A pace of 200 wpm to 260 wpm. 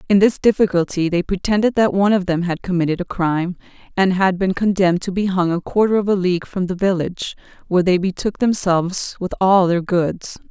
Yes: fast, 205 wpm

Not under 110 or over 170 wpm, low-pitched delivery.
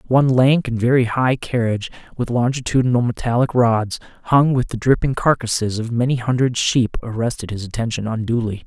Yes: average, 160 wpm; low, 120 Hz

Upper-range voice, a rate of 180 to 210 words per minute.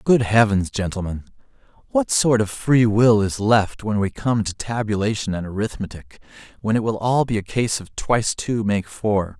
No: low, 110 Hz; average, 185 wpm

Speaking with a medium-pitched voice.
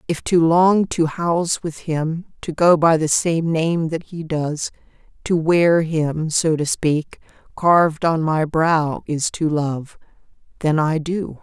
Yes: medium, 160 Hz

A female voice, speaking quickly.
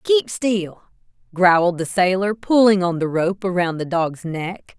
No: female; average, 165 wpm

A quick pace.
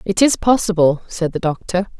No: average, 180 wpm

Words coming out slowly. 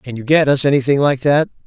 No: fast, 250 wpm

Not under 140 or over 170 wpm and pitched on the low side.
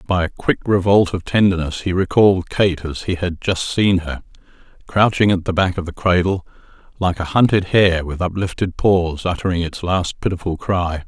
No: average, 185 wpm; very low, 90 Hz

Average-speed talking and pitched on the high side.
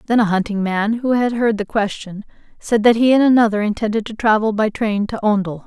No: fast, 220 wpm; high, 215 Hz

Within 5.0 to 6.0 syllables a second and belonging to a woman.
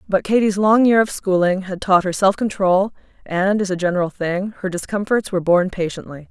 Yes: 5.5 syllables/s; female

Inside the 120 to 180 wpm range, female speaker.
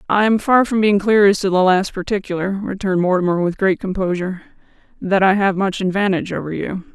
No: average, 200 wpm; female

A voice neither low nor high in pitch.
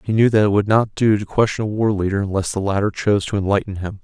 No: low, 105 Hz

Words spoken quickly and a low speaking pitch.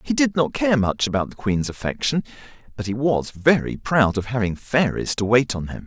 Yes: fast, 215 wpm; low, 125 Hz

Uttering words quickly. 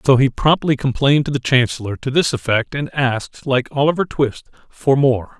No: average, 190 wpm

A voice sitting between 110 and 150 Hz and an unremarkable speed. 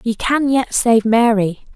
No: high, 230 Hz; average, 170 wpm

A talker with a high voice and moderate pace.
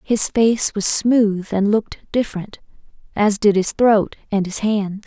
Yes: high, 210 Hz; average, 165 wpm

